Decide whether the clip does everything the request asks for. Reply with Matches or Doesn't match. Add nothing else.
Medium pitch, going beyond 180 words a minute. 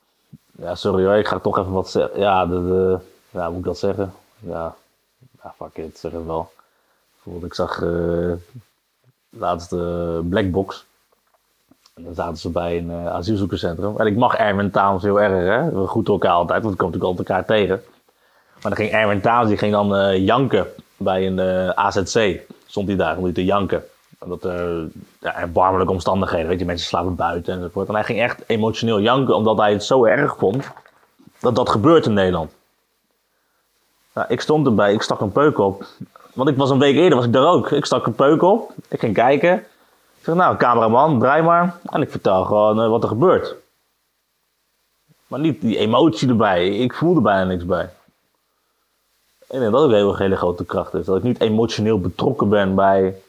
Doesn't match